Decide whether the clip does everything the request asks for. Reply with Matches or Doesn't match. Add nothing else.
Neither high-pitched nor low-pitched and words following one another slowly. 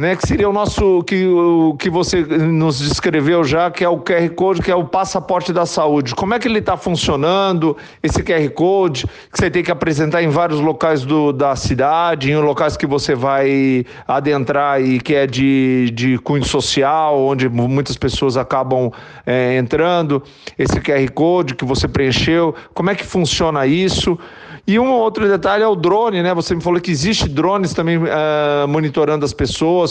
Doesn't match